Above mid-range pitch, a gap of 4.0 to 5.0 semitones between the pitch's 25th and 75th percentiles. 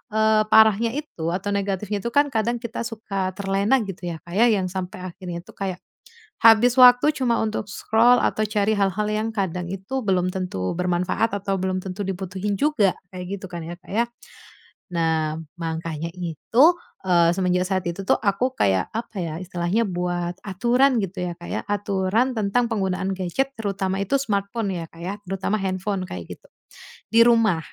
No: high, 195 Hz; average, 3.4 semitones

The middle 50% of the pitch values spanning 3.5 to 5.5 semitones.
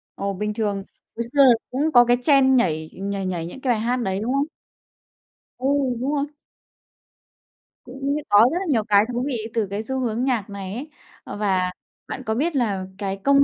Yes: average, 4.7 semitones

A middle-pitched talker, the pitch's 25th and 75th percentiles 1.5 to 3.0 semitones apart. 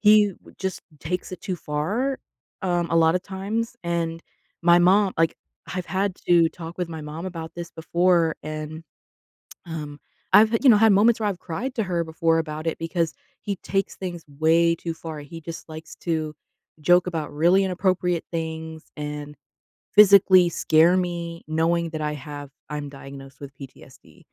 Yes: medium, 170 Hz; average, 2.7 semitones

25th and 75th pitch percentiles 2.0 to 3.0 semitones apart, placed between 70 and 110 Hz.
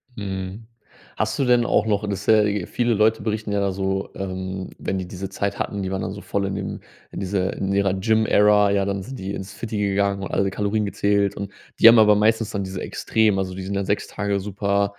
No: narrow, 1.5 semitones; low, 100 Hz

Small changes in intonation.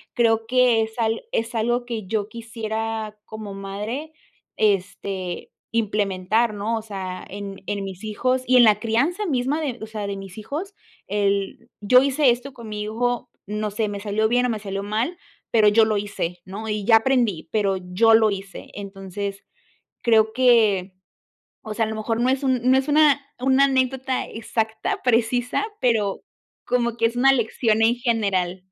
No: average, 3.2 semitones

